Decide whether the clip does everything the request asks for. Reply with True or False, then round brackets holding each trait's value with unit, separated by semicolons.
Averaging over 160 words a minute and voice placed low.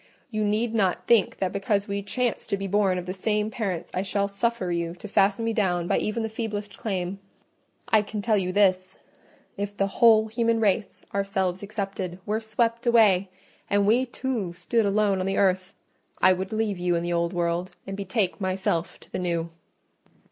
False (190 wpm; 200 Hz)